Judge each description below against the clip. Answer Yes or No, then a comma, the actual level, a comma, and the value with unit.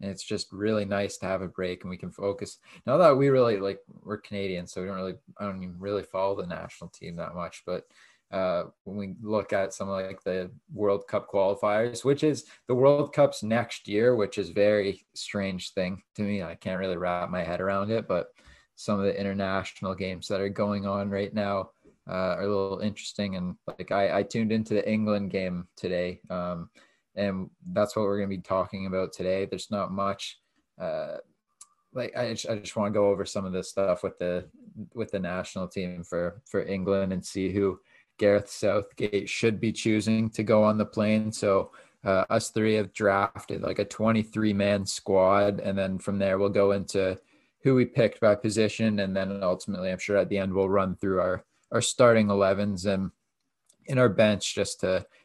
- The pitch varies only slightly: Yes, narrow, 1.9 semitones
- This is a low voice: Yes, low, 100 Hz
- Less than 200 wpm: No, fast, 205 wpm